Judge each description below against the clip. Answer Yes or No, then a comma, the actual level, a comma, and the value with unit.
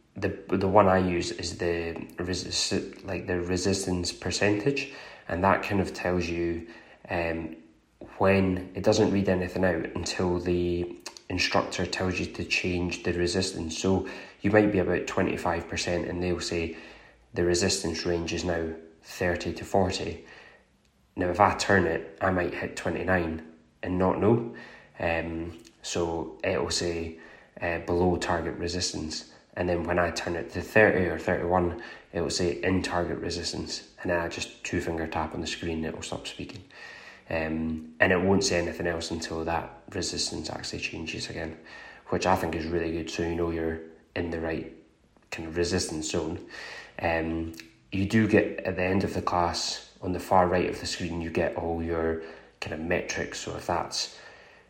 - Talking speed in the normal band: Yes, average, 180 wpm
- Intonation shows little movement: Yes, narrow, 1.9 semitones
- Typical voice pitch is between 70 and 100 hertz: Yes, very low, 85 Hz